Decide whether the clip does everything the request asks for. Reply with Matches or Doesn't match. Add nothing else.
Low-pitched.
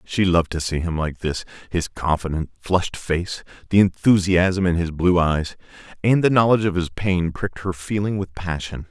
Matches